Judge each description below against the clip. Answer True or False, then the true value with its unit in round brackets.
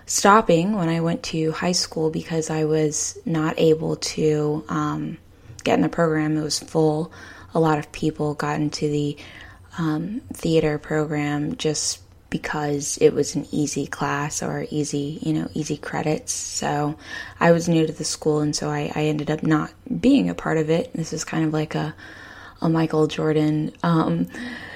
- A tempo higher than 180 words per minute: False (175 wpm)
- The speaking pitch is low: False (155 Hz)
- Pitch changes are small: True (1.2 semitones)